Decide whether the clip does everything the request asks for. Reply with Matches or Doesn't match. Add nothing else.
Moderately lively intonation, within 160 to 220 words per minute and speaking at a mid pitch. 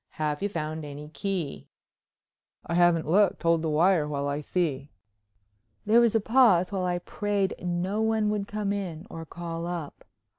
Matches